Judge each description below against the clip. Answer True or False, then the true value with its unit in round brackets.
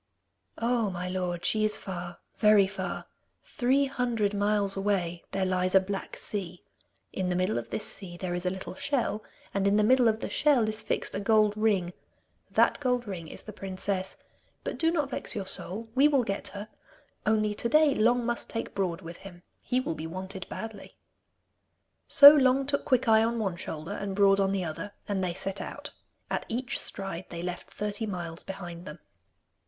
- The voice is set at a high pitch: True (200 Hz)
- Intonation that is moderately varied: True (3.6 semitones)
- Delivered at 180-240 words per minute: True (190 wpm)